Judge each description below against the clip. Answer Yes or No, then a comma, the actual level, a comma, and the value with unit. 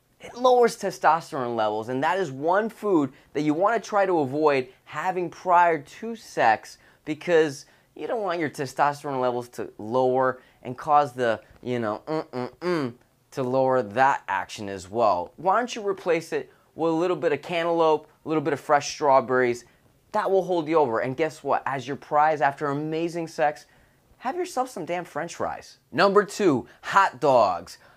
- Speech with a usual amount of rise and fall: Yes, average, 4.9 semitones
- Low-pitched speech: No, medium, 150 Hz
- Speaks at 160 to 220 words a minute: Yes, average, 180 wpm